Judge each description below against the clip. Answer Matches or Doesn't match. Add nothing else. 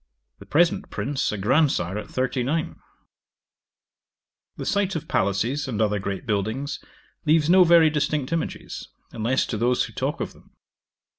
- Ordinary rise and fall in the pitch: Doesn't match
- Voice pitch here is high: Doesn't match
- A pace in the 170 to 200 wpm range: Doesn't match